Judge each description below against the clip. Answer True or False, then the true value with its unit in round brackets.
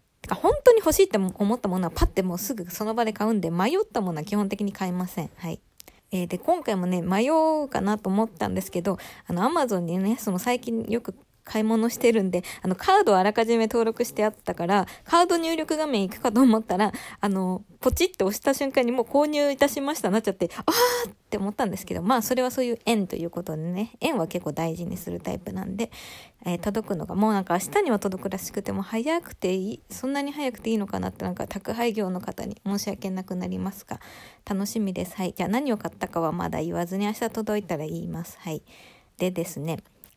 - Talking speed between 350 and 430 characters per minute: False (440 characters per minute)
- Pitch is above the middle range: True (210 Hz)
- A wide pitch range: False (4.4 semitones)